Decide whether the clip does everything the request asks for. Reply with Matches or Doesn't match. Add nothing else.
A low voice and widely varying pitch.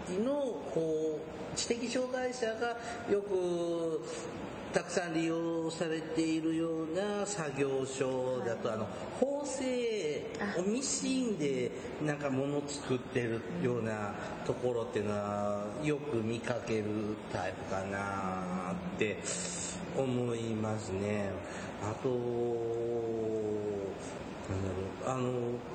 Matches